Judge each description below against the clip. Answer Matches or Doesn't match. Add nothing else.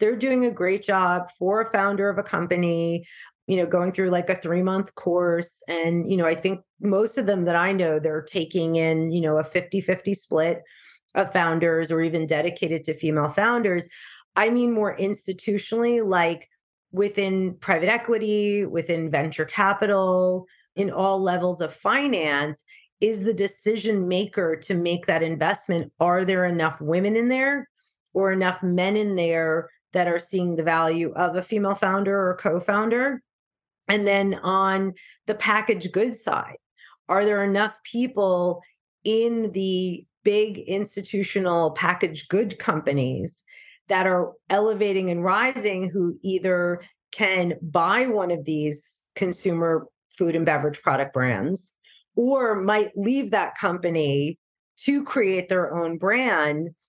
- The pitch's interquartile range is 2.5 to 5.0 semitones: Matches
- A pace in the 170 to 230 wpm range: Doesn't match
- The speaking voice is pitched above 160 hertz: Matches